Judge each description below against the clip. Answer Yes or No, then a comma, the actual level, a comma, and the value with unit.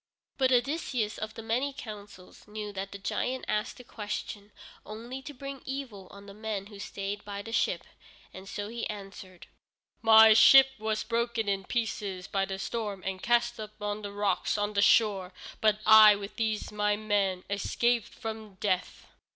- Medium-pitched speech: No, high, 210 Hz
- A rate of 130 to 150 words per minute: No, average, 175 wpm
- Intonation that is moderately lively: No, narrow, 2.2 semitones